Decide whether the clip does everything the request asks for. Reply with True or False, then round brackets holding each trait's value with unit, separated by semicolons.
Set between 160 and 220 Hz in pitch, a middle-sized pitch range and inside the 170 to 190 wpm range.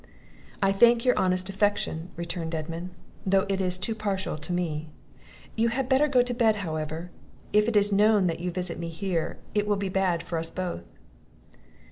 True (190 Hz; 3.8 semitones; 185 wpm)